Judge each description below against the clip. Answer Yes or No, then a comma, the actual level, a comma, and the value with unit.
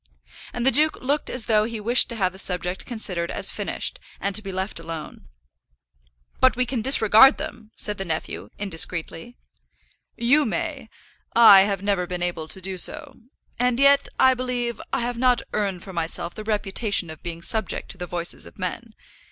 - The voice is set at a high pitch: Yes, high, 215 Hz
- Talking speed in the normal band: Yes, average, 185 wpm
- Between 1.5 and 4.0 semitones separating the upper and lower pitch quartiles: No, average, 5.2 semitones